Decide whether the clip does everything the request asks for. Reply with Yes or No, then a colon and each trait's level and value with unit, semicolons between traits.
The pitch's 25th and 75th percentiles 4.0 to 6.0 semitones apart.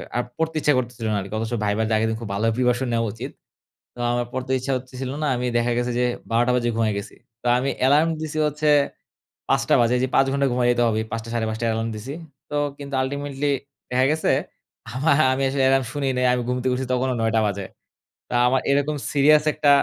No: average, 3.2 semitones